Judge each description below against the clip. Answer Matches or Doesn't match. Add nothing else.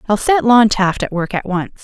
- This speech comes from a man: Doesn't match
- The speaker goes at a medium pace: Doesn't match